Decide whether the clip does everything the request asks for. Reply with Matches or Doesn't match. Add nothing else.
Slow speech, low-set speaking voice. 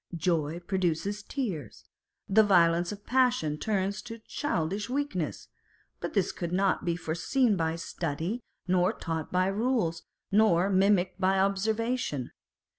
Doesn't match